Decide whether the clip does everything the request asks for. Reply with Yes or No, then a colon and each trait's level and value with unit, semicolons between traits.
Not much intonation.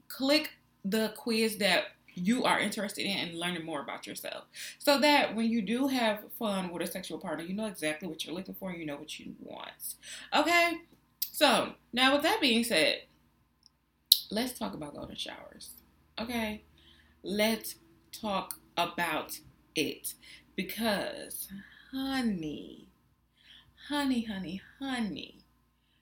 No: average, 4.8 semitones